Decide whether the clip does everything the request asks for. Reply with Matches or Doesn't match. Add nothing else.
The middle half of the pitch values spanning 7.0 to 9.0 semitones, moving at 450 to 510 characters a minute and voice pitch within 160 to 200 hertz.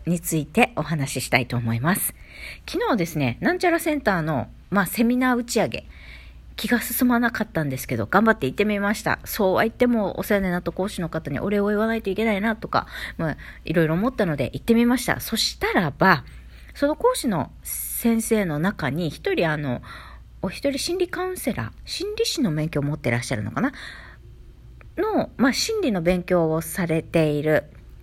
Doesn't match